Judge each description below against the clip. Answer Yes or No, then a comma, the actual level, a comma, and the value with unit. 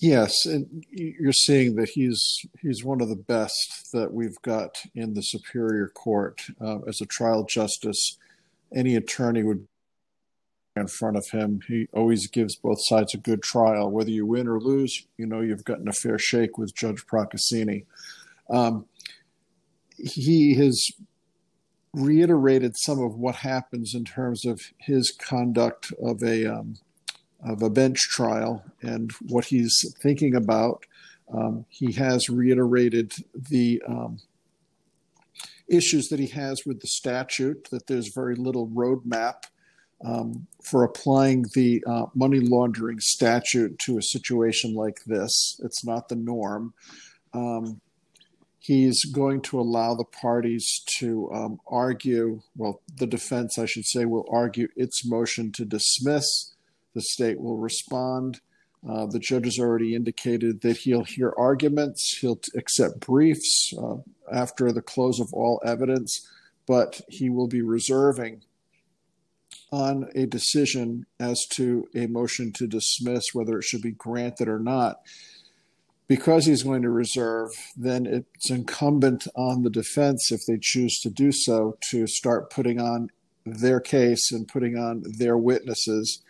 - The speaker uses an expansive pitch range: No, narrow, 2.5 semitones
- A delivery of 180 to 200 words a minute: No, average, 145 wpm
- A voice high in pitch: No, low, 120 Hz